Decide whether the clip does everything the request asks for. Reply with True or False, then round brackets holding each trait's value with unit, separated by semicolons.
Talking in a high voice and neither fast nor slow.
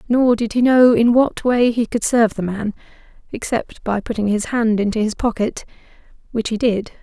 True (225 Hz; 190 wpm)